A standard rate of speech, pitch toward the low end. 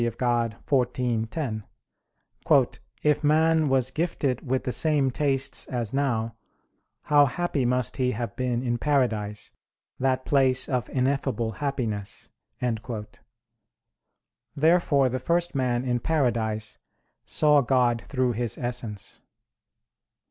No: slow, 110 wpm; low, 130 Hz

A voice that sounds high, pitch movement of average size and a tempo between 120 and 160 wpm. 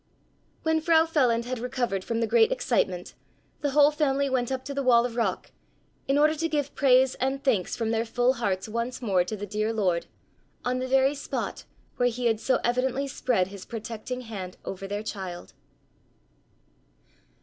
No: high, 245 Hz; average, 3.8 semitones; average, 180 wpm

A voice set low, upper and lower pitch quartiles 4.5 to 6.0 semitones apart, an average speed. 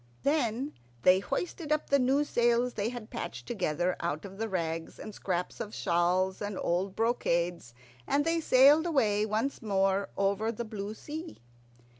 No: high, 215 Hz; average, 5.3 semitones; average, 160 wpm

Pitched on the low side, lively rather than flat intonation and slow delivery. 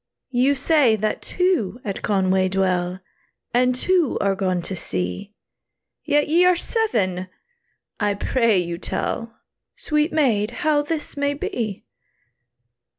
No: high, 230 Hz; wide, 7.5 semitones; slow, 125 wpm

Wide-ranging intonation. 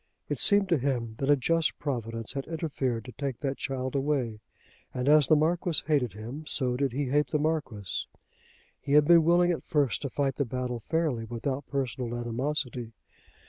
No: average, 3.5 semitones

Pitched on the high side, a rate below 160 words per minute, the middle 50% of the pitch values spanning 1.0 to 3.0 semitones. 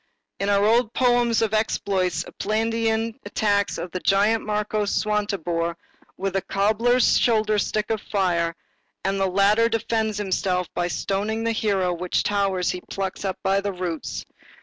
Yes: high, 205 Hz; average, 150 wpm; average, 2.7 semitones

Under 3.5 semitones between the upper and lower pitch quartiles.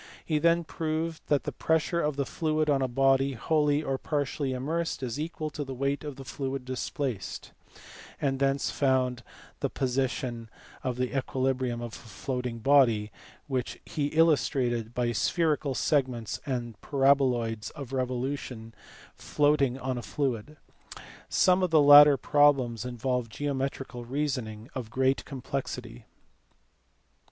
Yes: average, 2.9 semitones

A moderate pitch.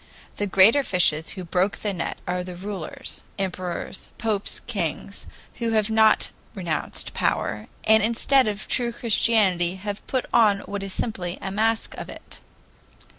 No: high, 200 Hz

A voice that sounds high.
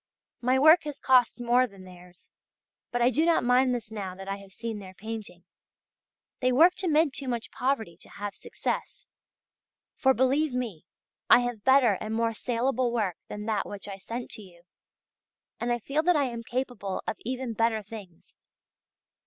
Yes: high, 235 Hz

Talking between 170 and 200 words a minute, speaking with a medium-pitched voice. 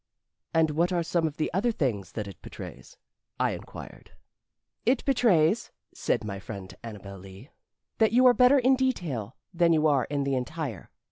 Yes: average, 175 wpm; medium, 155 Hz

